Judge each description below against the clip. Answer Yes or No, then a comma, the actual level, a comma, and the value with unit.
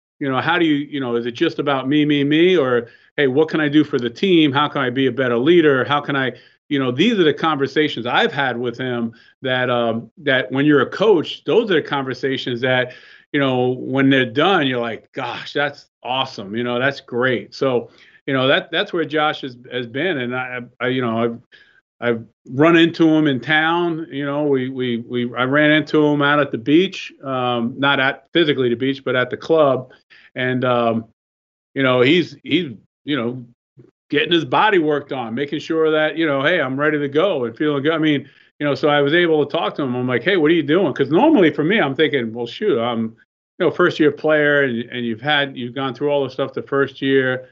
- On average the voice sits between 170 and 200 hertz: No, low, 135 Hz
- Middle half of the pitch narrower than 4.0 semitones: Yes, average, 3.3 semitones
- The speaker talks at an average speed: No, fast, 235 wpm